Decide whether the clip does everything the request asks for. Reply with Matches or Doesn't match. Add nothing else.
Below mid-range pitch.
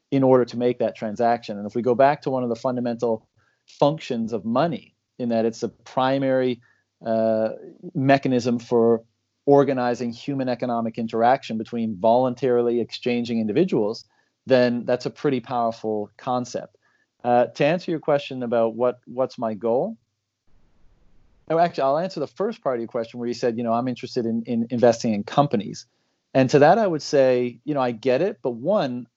Matches